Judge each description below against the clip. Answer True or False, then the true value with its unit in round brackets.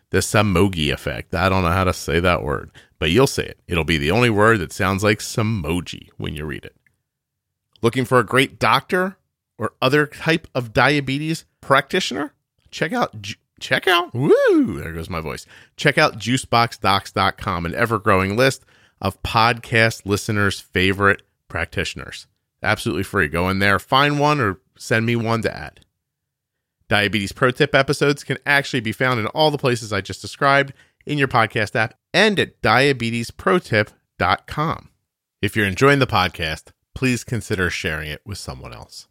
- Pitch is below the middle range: True (110 Hz)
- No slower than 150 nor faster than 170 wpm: True (165 wpm)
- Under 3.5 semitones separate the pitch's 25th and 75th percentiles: False (5.6 semitones)